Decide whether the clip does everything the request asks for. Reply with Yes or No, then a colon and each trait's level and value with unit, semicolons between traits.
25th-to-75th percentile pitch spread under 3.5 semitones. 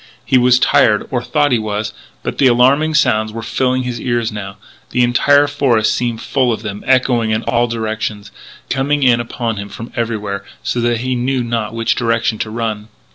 Yes: narrow, 2.6 semitones